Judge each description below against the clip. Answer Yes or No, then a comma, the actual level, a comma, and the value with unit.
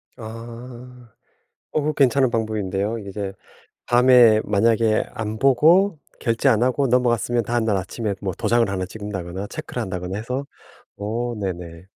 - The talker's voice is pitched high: No, low, 115 Hz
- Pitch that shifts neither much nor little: Yes, average, 3.4 semitones